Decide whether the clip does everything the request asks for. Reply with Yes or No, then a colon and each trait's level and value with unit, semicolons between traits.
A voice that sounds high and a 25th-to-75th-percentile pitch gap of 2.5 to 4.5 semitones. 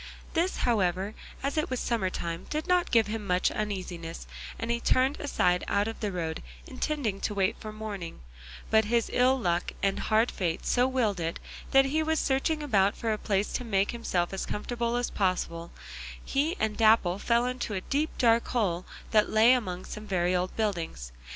No: high, 215 Hz; average, 5.0 semitones